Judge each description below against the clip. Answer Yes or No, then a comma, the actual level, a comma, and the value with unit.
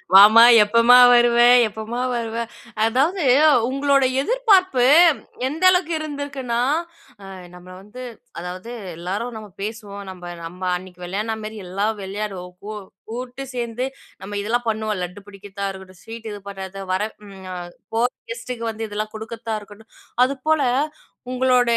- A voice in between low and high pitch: No, high, 225 Hz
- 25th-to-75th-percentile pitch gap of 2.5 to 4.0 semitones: Yes, average, 3.7 semitones